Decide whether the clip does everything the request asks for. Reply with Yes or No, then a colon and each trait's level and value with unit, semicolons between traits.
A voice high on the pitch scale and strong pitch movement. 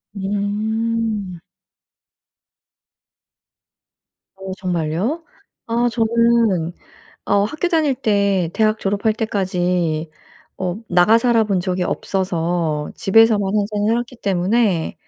No: high, 205 Hz; average, 3.9 semitones